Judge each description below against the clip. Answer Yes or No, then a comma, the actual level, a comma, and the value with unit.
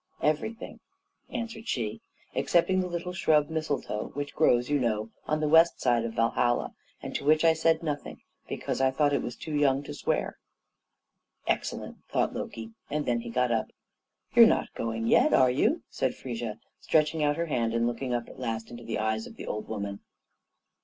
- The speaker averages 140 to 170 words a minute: No, average, 185 wpm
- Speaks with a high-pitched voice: No, low, 135 Hz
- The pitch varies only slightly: No, average, 5.2 semitones